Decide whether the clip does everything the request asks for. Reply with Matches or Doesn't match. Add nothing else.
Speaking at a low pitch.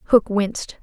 Doesn't match